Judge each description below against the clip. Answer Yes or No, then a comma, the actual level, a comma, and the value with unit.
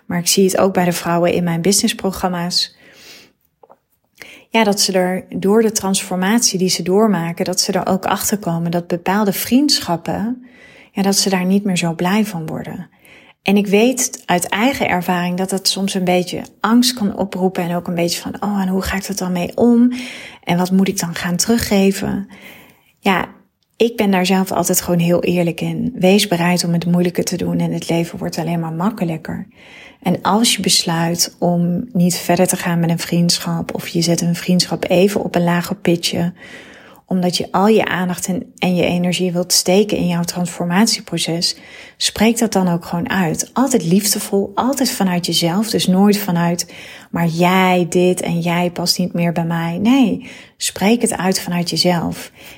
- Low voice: No, medium, 185 Hz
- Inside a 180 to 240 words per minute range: Yes, average, 185 wpm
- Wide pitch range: No, average, 2.8 semitones